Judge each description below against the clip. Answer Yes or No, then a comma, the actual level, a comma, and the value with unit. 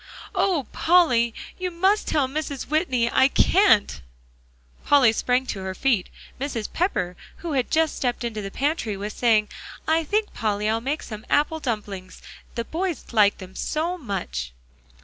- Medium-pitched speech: No, very high, 255 Hz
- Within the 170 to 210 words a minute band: No, average, 155 wpm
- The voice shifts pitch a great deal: Yes, wide, 7.0 semitones